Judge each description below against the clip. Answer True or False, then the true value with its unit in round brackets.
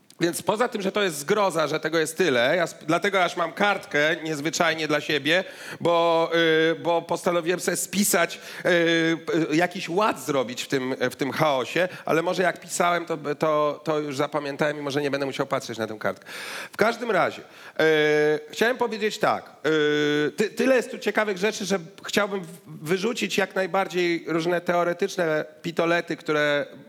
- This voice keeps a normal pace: False (170 wpm)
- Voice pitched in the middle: True (170 Hz)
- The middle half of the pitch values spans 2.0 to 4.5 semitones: True (3.8 semitones)